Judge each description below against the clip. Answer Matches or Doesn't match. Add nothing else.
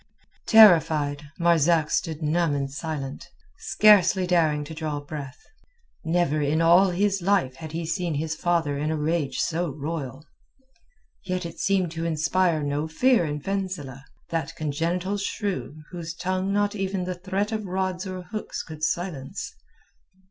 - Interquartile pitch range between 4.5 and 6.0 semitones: Doesn't match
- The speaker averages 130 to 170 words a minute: Matches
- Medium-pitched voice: Matches